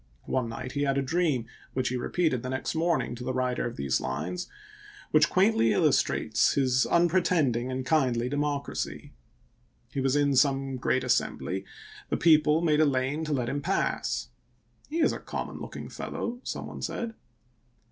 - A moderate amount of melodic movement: Yes, average, 3.8 semitones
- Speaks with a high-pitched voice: No, low, 135 Hz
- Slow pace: No, average, 175 wpm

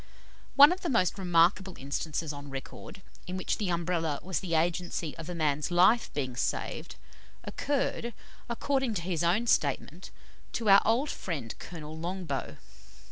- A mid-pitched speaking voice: Yes, medium, 175 Hz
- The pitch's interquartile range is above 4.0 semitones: Yes, average, 4.4 semitones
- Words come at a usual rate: Yes, average, 150 wpm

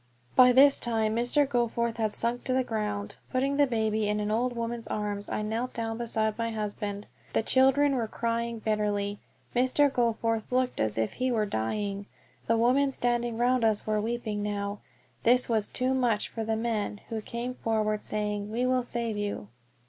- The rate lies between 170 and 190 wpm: Yes, average, 180 wpm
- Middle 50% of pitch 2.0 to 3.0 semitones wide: Yes, narrow, 2.5 semitones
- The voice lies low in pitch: No, high, 225 Hz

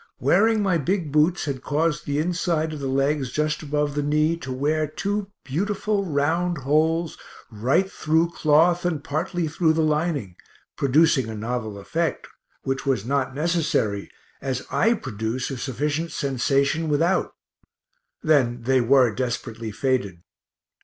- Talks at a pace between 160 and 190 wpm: No, average, 140 wpm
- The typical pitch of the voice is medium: Yes, medium, 150 Hz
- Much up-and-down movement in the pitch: No, average, 4.0 semitones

